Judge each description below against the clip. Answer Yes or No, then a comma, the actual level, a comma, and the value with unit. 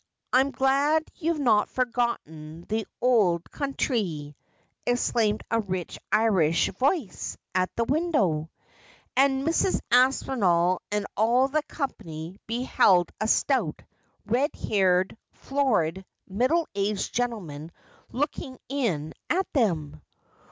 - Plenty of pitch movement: Yes, wide, 7.0 semitones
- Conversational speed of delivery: No, slow, 105 wpm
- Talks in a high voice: Yes, high, 225 Hz